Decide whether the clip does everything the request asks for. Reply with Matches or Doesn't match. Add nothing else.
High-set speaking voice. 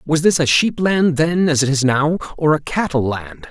Doesn't match